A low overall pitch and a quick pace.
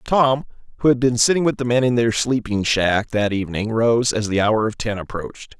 Yes: low, 115 Hz; fast, 225 wpm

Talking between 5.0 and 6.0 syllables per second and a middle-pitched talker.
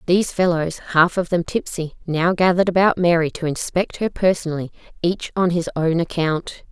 Yes: 5.2 syllables/s; medium, 170 Hz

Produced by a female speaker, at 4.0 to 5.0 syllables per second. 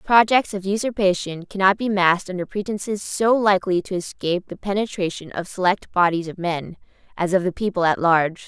No: female; 5.6 syllables/s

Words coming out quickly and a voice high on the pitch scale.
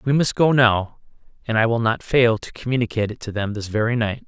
No: fast, 240 wpm; low, 115 Hz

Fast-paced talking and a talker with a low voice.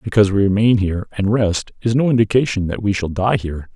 Yes: fast, 225 wpm; low, 105 Hz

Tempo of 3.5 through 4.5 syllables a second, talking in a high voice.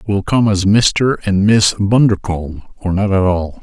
No: 4.4 syllables/s; low, 100 Hz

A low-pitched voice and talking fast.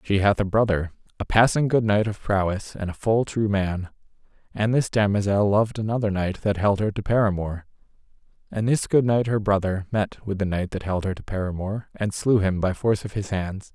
Yes: low, 100 Hz; fast, 215 wpm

